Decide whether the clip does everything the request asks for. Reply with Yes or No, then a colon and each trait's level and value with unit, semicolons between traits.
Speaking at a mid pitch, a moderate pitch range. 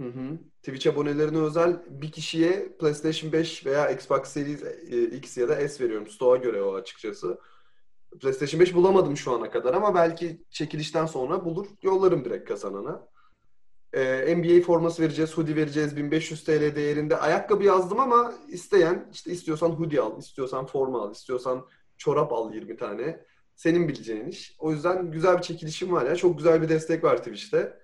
Yes: medium, 165 Hz; average, 3.5 semitones